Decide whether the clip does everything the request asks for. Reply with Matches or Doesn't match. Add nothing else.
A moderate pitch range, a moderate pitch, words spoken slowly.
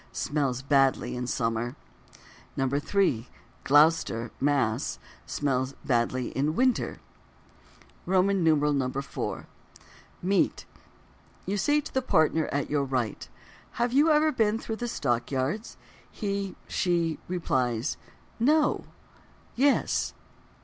Doesn't match